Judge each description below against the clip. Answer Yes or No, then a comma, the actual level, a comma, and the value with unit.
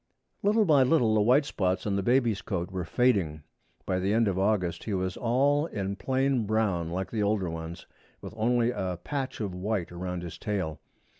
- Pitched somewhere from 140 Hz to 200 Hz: No, low, 105 Hz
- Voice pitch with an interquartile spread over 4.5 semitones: Yes, average, 5.0 semitones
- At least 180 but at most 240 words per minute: Yes, average, 195 wpm